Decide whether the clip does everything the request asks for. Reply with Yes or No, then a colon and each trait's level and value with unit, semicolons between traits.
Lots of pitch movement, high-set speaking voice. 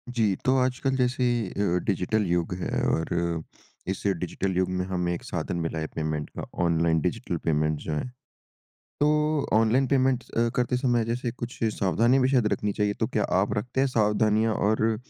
No: wide, 6.0 semitones; low, 110 Hz